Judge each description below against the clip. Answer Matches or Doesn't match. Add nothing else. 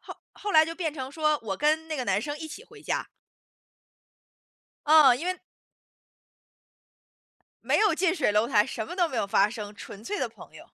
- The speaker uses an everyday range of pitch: Doesn't match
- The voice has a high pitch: Matches